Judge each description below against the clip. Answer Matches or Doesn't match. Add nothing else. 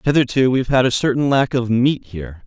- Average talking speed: Doesn't match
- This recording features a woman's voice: Doesn't match